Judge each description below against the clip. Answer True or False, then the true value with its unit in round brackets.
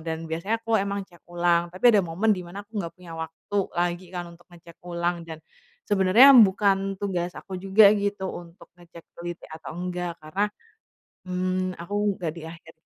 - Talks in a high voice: False (180 Hz)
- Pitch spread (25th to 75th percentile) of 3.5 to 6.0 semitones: False (2.4 semitones)